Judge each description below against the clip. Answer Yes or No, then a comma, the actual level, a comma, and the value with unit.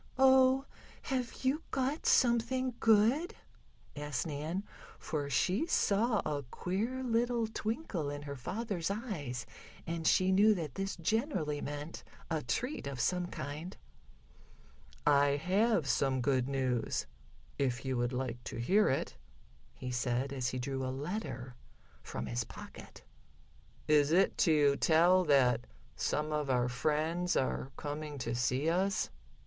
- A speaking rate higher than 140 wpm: No, slow, 135 wpm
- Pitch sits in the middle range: Yes, medium, 155 Hz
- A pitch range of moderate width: No, wide, 7.7 semitones